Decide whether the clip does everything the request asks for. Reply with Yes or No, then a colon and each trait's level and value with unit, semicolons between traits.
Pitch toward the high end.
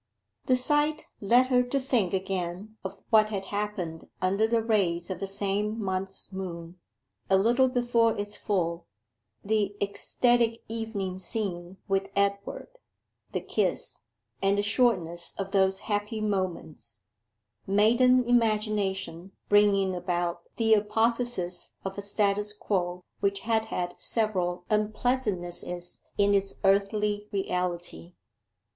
Yes: high, 200 Hz